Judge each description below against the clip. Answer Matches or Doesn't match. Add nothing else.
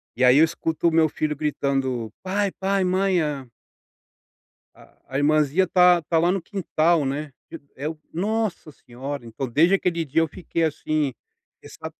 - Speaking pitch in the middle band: Matches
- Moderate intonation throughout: Matches